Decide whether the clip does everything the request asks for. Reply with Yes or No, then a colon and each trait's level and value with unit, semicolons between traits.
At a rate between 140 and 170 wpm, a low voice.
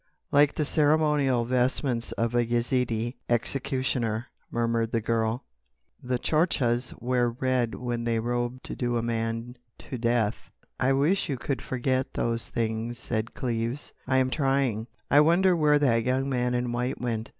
Yes: average, 155 wpm; low, 120 Hz